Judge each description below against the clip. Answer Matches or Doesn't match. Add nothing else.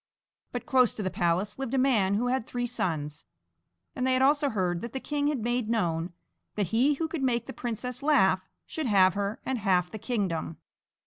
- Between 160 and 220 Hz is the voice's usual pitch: Doesn't match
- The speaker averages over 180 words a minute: Matches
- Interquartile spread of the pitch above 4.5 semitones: Matches